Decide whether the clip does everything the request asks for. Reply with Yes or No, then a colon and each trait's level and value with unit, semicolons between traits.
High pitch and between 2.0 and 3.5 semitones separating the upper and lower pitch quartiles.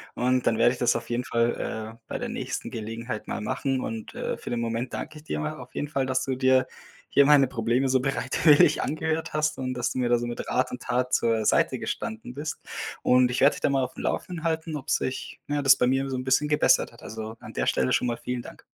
No: low, 130 Hz; average, 2.7 semitones